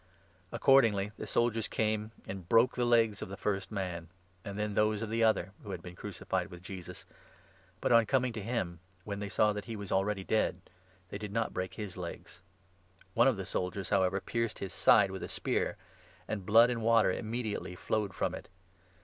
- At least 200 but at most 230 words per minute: Yes, fast, 205 wpm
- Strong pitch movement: No, average, 3.0 semitones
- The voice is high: No, low, 105 Hz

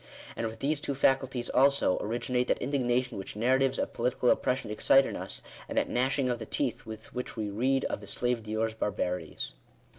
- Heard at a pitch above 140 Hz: No, low, 125 Hz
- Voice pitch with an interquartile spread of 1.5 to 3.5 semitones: Yes, average, 3.2 semitones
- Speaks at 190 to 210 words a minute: Yes, average, 200 wpm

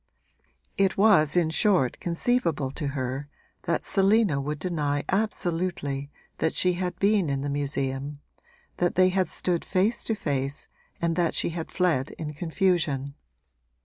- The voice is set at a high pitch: No, medium, 165 Hz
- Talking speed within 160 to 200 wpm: No, average, 145 wpm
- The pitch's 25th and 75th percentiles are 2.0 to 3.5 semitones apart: No, average, 4.6 semitones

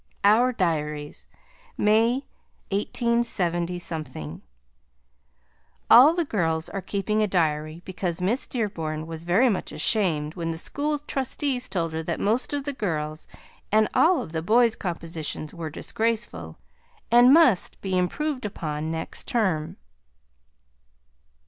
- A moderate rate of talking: No, slow, 125 wpm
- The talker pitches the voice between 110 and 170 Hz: No, medium, 185 Hz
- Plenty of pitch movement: Yes, wide, 6.6 semitones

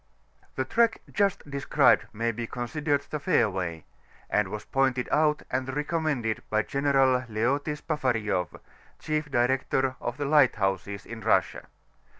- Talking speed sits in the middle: No, slow, 130 wpm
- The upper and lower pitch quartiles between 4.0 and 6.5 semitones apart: Yes, average, 4.7 semitones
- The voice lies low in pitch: Yes, low, 130 Hz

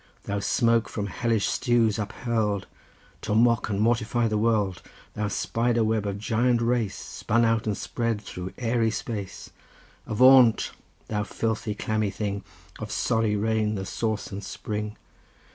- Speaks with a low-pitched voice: Yes, low, 110 Hz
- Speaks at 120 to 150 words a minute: Yes, average, 145 wpm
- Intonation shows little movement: Yes, narrow, 2.0 semitones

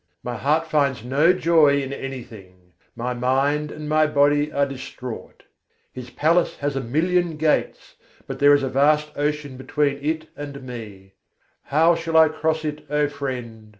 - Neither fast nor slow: Yes, average, 160 wpm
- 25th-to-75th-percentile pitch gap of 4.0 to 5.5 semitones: No, average, 2.9 semitones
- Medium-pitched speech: Yes, medium, 145 Hz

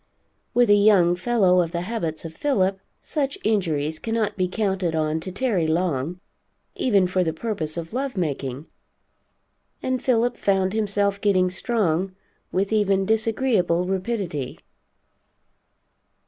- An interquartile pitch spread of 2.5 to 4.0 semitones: No, average, 4.4 semitones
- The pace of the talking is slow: Yes, slow, 130 wpm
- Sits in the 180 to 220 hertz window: Yes, high, 190 Hz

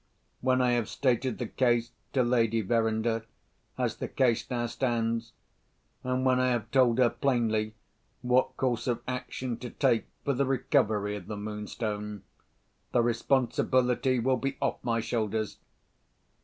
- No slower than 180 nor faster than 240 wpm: No, average, 145 wpm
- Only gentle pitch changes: Yes, narrow, 2.3 semitones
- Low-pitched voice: Yes, low, 120 Hz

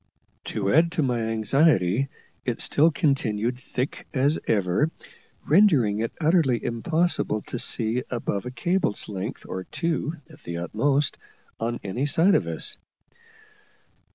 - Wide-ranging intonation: Yes, wide, 6.0 semitones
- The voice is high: No, low, 125 Hz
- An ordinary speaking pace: No, slow, 130 wpm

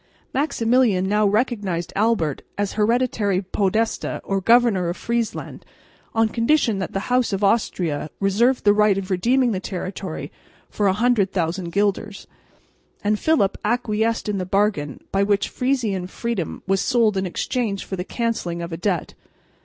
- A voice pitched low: No, high, 205 Hz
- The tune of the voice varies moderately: Yes, average, 3.4 semitones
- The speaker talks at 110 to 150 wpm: Yes, average, 145 wpm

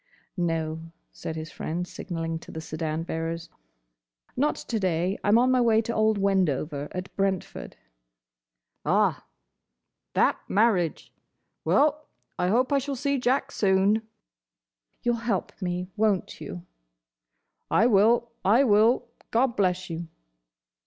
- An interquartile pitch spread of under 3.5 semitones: No, wide, 5.6 semitones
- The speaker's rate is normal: No, slow, 125 wpm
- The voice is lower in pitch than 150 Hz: No, high, 195 Hz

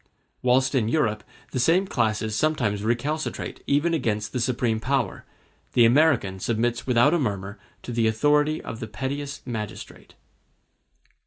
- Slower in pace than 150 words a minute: Yes, average, 140 wpm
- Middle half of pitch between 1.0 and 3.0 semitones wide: No, average, 4.6 semitones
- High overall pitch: No, low, 120 Hz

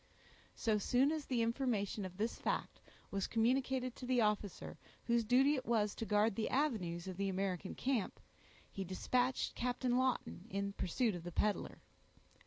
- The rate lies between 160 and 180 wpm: Yes, average, 165 wpm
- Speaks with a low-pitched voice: No, high, 225 Hz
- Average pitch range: Yes, average, 4.2 semitones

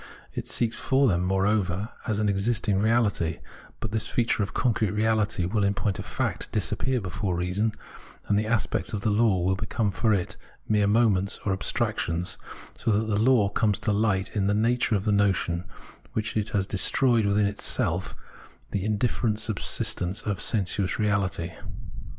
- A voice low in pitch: Yes, low, 105 Hz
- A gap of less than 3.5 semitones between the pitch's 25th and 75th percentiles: Yes, narrow, 2.4 semitones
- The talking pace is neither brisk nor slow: Yes, average, 165 wpm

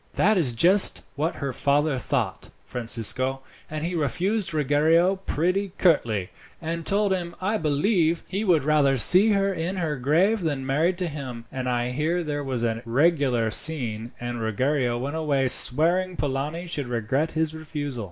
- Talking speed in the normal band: Yes, average, 160 wpm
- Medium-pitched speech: Yes, medium, 150 Hz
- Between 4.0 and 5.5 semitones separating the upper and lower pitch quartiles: Yes, average, 5.0 semitones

